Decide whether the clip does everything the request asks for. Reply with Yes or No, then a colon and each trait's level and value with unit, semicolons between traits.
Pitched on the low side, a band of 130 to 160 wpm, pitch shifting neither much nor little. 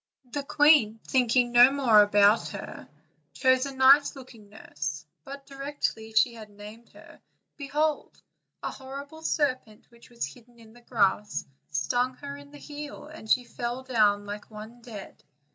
No: high, 245 Hz; average, 155 wpm; average, 4.3 semitones